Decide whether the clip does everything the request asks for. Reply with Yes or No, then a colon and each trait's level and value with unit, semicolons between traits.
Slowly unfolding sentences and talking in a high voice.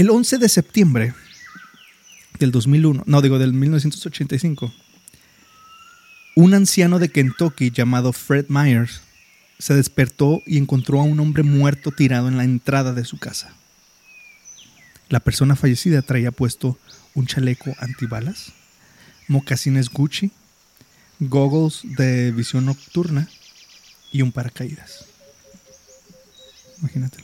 No: slow, 110 wpm; medium, 140 Hz